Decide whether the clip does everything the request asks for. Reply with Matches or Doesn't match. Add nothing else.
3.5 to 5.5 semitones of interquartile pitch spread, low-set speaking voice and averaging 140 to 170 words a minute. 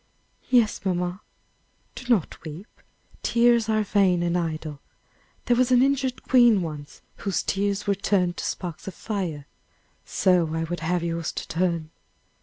Doesn't match